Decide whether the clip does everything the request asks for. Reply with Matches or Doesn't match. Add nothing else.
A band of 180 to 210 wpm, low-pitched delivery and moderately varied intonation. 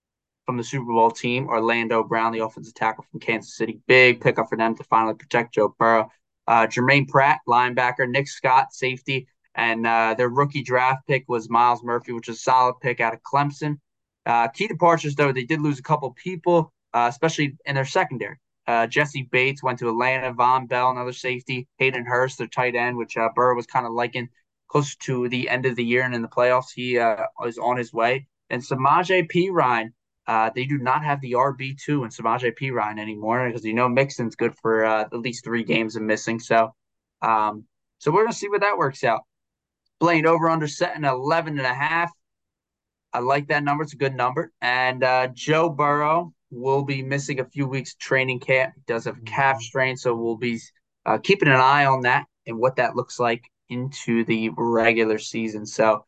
Matches